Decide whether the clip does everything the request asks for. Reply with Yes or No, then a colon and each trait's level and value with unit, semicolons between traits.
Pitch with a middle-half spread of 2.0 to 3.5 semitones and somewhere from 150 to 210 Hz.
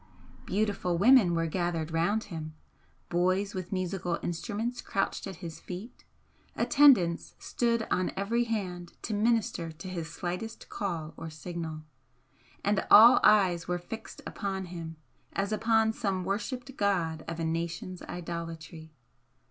No: average, 3.9 semitones; medium, 185 Hz